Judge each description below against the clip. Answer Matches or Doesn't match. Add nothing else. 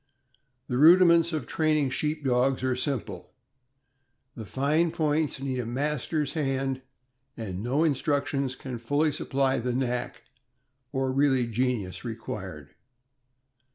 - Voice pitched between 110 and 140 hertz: Matches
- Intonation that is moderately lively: Matches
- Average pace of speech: Doesn't match